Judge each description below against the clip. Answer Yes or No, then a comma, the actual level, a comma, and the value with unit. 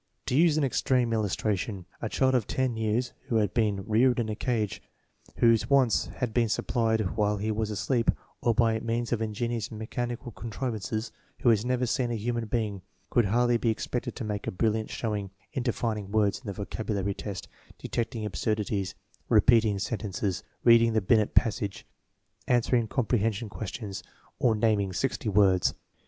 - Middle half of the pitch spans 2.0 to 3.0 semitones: Yes, narrow, 2.4 semitones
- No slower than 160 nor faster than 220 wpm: Yes, average, 170 wpm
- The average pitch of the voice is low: Yes, low, 110 Hz